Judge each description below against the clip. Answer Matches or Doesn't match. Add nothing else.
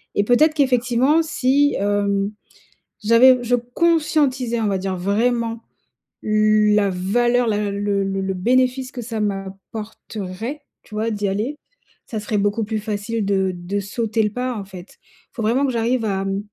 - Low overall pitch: Doesn't match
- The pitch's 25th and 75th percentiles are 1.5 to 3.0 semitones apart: Doesn't match